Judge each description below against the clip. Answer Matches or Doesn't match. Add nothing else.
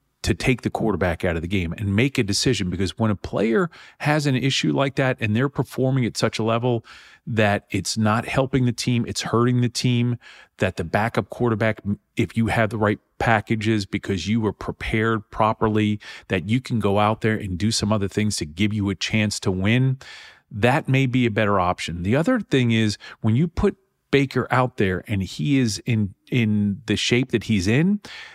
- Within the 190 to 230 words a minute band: Matches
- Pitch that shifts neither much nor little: Matches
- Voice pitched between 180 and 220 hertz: Doesn't match